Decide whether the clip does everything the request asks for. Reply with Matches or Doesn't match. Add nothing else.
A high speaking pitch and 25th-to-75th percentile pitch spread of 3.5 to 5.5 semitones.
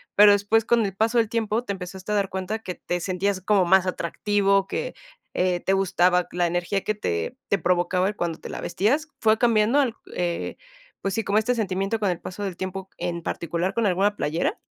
Doesn't match